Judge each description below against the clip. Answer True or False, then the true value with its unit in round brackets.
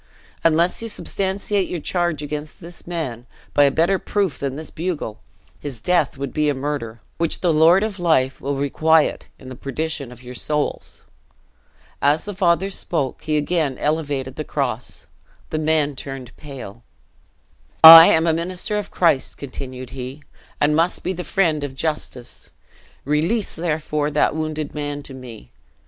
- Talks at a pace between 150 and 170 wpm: True (160 wpm)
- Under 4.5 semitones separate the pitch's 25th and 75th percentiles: True (3.7 semitones)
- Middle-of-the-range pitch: True (150 Hz)